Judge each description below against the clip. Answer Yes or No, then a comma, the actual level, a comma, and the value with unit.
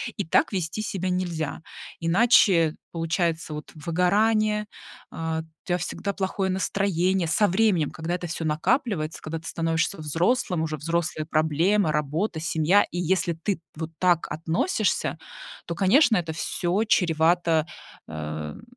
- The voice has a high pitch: No, medium, 170 Hz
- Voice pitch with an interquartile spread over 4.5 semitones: No, average, 3.2 semitones